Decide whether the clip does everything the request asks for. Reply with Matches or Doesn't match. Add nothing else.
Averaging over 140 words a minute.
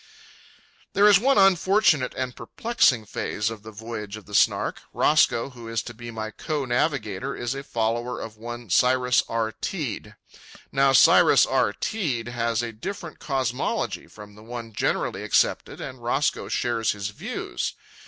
Matches